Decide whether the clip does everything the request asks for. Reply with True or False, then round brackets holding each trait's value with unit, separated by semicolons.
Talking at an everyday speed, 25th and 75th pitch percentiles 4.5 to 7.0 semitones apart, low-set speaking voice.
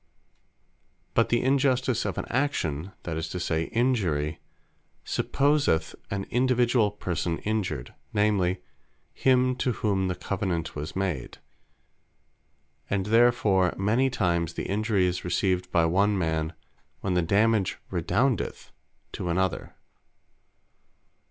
False (115 wpm; 5.2 semitones; 95 Hz)